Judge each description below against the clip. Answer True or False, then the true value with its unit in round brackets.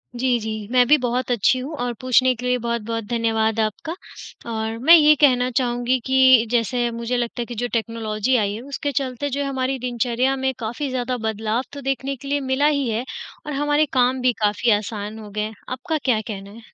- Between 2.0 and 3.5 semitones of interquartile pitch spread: True (2.6 semitones)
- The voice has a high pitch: True (245 Hz)